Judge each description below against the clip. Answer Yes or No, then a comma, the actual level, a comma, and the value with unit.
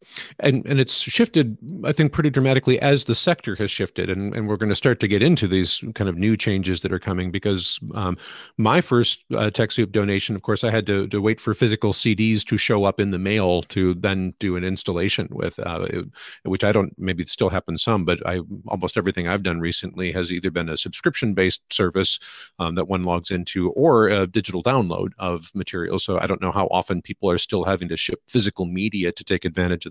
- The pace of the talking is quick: Yes, fast, 220 wpm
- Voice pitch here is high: No, low, 100 Hz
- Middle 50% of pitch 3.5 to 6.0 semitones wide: No, average, 3.1 semitones